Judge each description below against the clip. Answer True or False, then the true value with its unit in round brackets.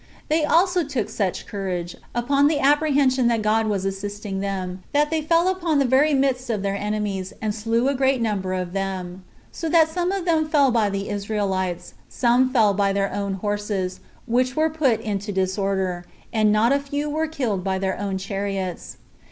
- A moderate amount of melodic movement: False (6.3 semitones)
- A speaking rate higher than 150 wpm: True (185 wpm)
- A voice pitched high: True (215 Hz)